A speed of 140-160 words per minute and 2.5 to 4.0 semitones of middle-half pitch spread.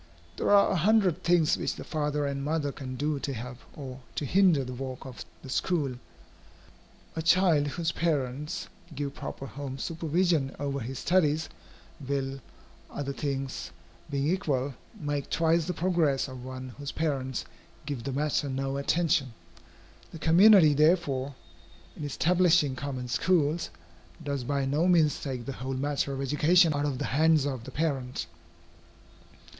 Yes: average, 150 wpm; average, 3.2 semitones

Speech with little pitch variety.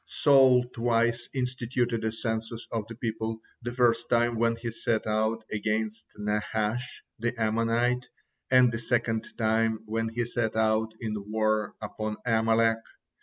Yes: narrow, 1.4 semitones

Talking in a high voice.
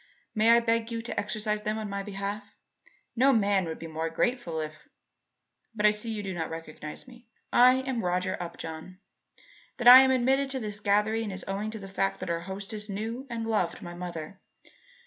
Yes: high, 210 Hz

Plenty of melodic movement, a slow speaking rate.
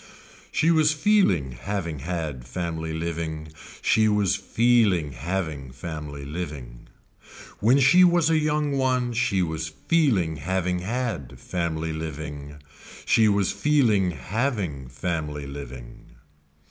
Yes: wide, 7.6 semitones; slow, 115 wpm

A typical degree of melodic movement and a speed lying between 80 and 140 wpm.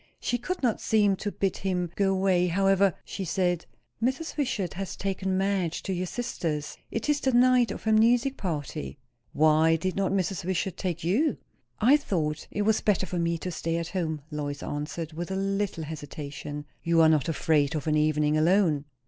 No: average, 4.1 semitones; average, 190 wpm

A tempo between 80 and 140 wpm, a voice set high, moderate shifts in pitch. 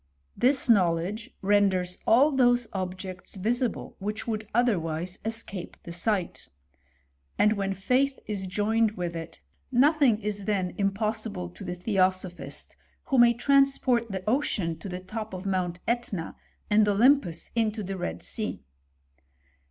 Yes: slow, 135 wpm; high, 205 Hz; average, 4.1 semitones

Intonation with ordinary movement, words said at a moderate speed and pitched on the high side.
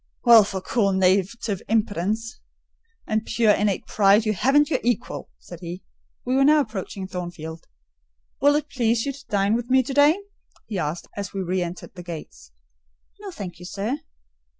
Yes: average, 4.8 semitones; average, 175 wpm; high, 210 Hz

